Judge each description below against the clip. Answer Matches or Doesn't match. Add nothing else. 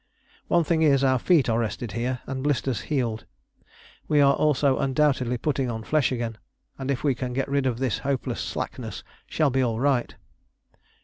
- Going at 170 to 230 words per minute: Matches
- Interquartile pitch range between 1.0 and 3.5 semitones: Matches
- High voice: Doesn't match